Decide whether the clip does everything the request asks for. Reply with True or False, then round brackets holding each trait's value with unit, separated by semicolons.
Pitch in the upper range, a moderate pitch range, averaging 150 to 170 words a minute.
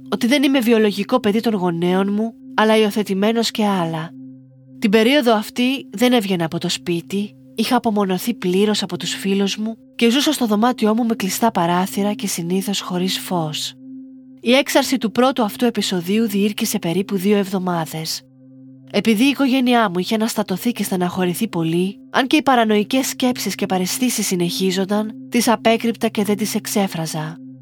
True (210 Hz; 4.4 semitones; 155 wpm)